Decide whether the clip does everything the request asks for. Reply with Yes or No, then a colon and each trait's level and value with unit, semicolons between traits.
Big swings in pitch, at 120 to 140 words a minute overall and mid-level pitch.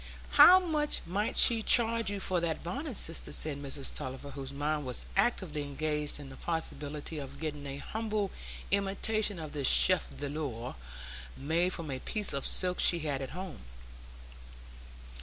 No: wide, 5.8 semitones; average, 160 wpm; medium, 160 Hz